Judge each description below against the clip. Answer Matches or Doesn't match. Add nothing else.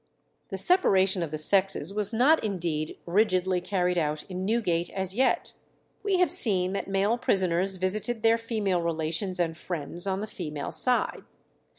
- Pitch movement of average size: Matches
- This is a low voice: Doesn't match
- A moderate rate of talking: Matches